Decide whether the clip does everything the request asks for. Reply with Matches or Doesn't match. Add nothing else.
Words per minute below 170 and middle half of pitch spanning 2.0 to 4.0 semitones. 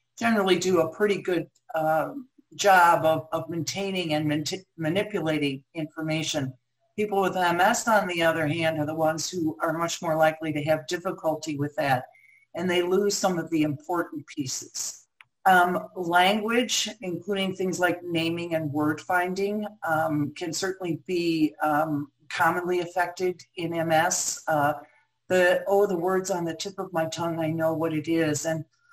Matches